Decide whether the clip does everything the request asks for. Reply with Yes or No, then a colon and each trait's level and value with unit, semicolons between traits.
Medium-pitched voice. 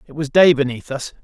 Yes: medium, 145 Hz